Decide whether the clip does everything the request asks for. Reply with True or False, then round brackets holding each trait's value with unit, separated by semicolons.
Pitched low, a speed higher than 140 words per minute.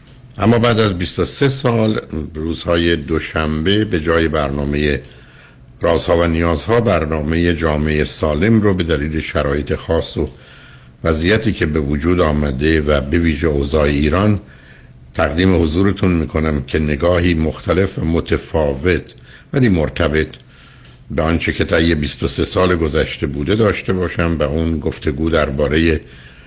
False (80 Hz; 125 wpm)